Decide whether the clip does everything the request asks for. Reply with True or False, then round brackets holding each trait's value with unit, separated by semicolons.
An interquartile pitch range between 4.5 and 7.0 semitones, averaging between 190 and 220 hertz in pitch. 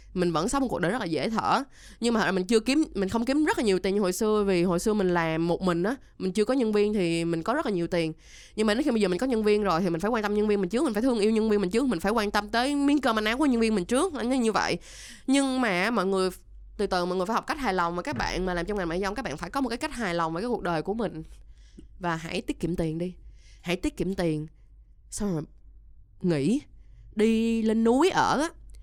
True (4.8 semitones; 205 Hz)